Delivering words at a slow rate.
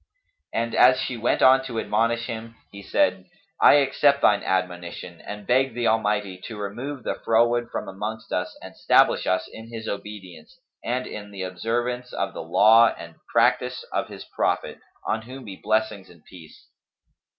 No: average, 170 wpm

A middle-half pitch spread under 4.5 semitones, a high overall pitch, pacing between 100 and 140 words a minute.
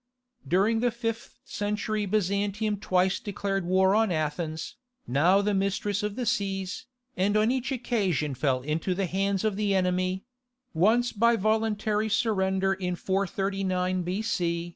Yes: average, 2.7 semitones; high, 195 Hz; slow, 135 wpm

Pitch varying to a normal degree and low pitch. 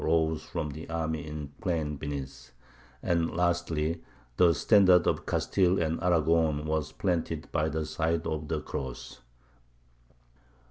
No: narrow, 1.8 semitones; very low, 80 Hz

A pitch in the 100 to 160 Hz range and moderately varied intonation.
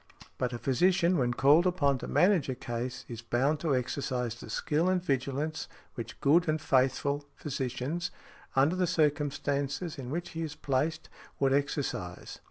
Yes: medium, 140 Hz; average, 3.8 semitones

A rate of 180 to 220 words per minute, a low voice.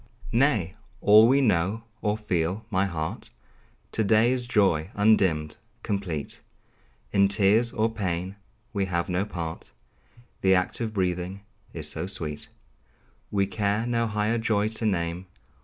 No: average, 140 wpm; low, 100 Hz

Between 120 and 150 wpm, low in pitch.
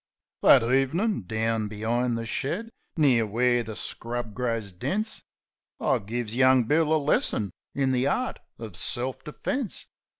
Yes: average, 140 wpm; low, 120 Hz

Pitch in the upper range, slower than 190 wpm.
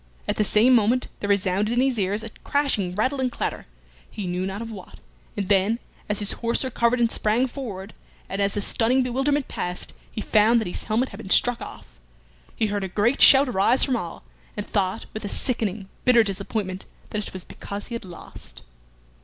No: high, 215 Hz; fast, 205 wpm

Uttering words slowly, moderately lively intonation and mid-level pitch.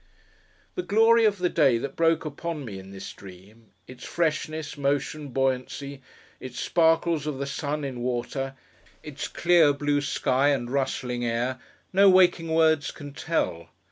No: average, 150 wpm; average, 4.1 semitones; medium, 145 Hz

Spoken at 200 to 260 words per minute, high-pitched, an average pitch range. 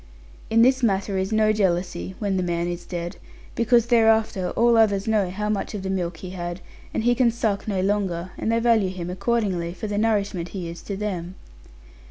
Yes: fast, 205 wpm; high, 200 Hz; average, 3.5 semitones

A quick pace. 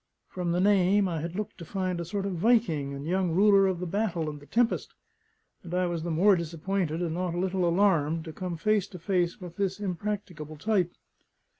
Yes: fast, 210 wpm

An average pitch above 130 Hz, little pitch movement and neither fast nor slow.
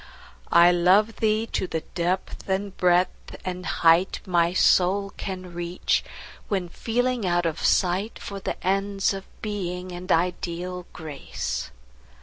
No: medium, 185 Hz; narrow, 2.1 semitones; slow, 130 wpm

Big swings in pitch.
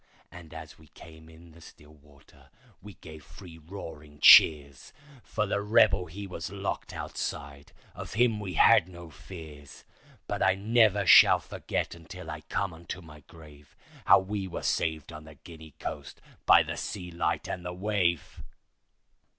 No: average, 3.6 semitones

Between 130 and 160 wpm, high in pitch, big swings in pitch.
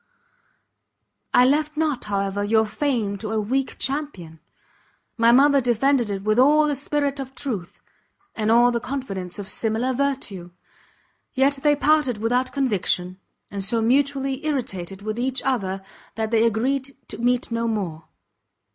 No: average, 145 wpm; high, 240 Hz; average, 4.7 semitones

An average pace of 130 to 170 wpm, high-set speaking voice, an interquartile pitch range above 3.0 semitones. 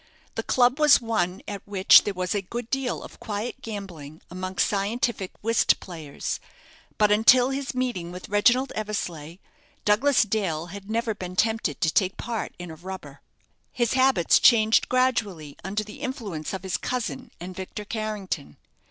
Yes: average, 160 wpm; high, 210 Hz; average, 4.4 semitones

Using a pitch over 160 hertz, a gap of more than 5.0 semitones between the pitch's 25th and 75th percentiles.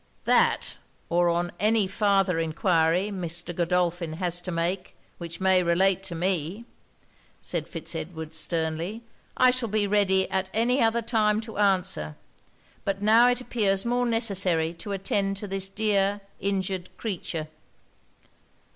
No: high, 190 Hz; average, 3.4 semitones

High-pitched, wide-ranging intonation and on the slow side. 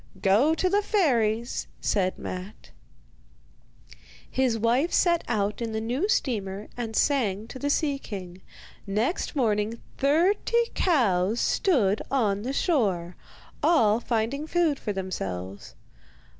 Yes: high, 230 Hz; wide, 6.3 semitones; slow, 120 wpm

